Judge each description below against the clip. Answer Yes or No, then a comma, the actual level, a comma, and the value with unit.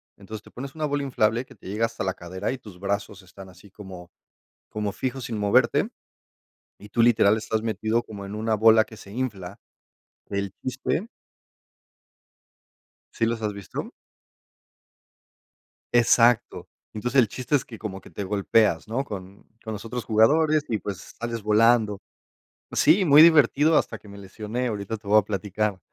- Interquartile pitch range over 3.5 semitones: No, average, 3.1 semitones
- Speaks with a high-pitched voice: No, low, 110 Hz